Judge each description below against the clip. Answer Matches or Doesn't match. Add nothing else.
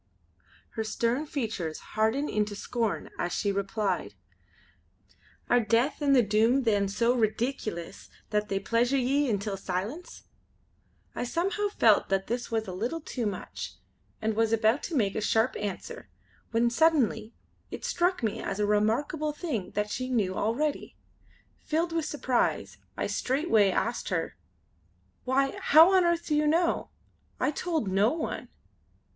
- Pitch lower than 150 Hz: Doesn't match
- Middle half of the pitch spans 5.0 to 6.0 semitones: Matches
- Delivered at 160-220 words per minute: Doesn't match